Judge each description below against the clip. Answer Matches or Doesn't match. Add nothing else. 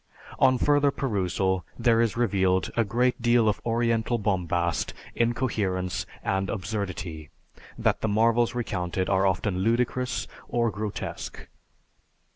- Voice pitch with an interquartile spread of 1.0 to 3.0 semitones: Doesn't match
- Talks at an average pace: Doesn't match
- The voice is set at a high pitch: Doesn't match